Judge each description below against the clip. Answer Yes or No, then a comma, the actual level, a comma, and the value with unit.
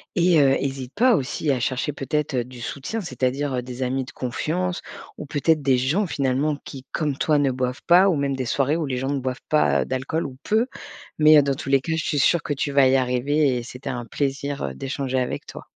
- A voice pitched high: No, medium, 140 Hz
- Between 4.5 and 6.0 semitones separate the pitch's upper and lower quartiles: No, average, 2.9 semitones